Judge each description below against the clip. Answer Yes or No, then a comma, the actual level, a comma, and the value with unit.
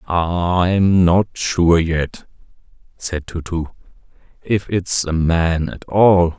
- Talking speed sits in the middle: No, slow, 120 wpm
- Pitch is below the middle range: Yes, very low, 85 Hz